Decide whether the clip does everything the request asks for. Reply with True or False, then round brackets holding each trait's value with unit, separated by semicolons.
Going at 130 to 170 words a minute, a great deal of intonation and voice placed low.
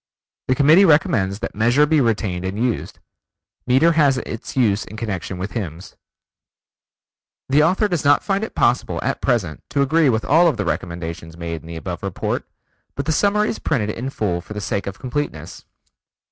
False (180 wpm; 7.6 semitones; 120 Hz)